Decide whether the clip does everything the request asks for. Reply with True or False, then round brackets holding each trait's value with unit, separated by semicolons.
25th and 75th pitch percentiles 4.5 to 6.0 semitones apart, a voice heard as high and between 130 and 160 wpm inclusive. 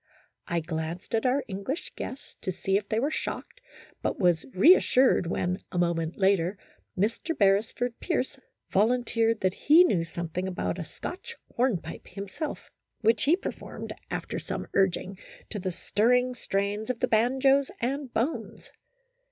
True (5.6 semitones; 210 Hz; 150 wpm)